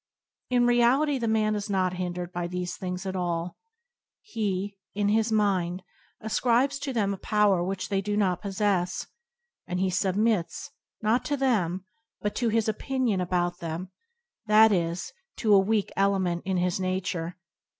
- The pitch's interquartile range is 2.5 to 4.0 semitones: Yes, average, 3.3 semitones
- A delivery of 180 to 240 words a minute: No, average, 160 wpm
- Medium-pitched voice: No, high, 195 Hz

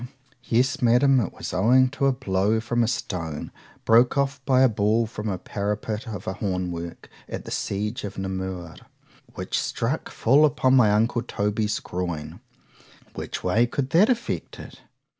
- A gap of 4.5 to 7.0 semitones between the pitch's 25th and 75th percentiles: Yes, average, 5.0 semitones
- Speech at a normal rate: Yes, average, 160 wpm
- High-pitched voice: No, low, 110 Hz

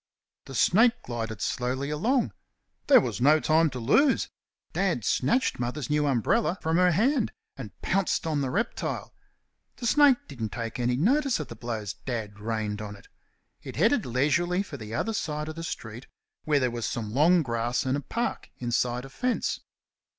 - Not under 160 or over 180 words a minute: Yes, average, 175 wpm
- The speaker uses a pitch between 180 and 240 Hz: No, medium, 140 Hz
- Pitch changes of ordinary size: No, wide, 7.1 semitones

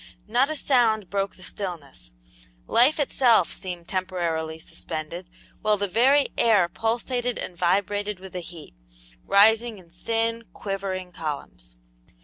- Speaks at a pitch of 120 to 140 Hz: No, high, 195 Hz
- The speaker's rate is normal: No, slow, 125 wpm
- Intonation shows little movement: No, average, 4.6 semitones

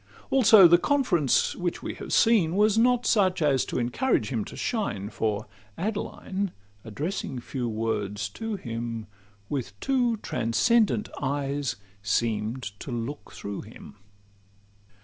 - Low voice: No, medium, 145 Hz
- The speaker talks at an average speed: No, slow, 130 wpm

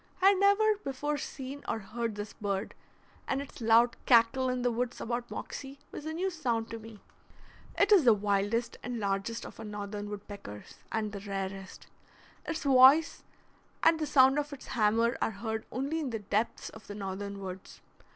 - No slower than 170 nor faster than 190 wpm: Yes, average, 180 wpm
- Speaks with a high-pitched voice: Yes, high, 230 Hz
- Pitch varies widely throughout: No, average, 4.9 semitones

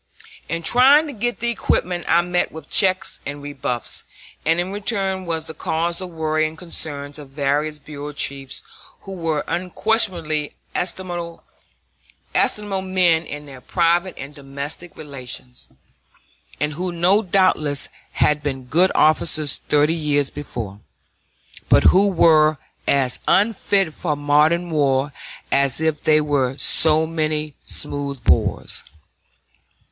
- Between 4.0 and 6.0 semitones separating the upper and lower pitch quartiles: No, average, 3.5 semitones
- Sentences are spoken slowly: Yes, slow, 125 wpm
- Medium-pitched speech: Yes, medium, 155 Hz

